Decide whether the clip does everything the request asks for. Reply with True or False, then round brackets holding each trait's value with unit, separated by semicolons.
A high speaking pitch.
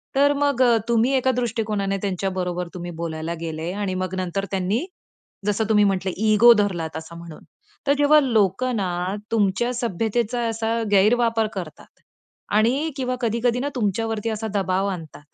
True (210 Hz)